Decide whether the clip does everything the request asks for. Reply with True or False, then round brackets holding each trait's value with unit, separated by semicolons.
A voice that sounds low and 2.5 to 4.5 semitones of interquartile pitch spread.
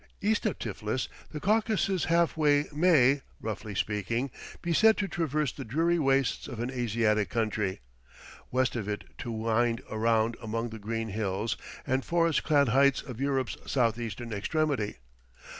False (125 Hz; 5.5 semitones)